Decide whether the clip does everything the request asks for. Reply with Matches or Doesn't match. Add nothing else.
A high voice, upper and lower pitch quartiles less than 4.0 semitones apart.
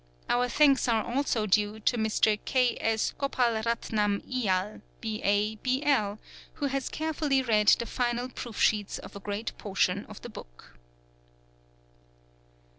Matches